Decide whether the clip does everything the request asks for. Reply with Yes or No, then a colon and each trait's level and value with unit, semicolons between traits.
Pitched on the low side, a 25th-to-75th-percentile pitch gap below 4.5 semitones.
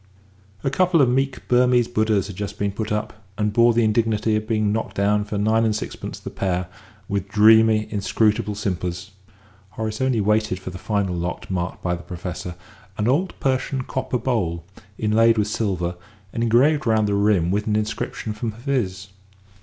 Yes: low, 105 Hz; narrow, 2.6 semitones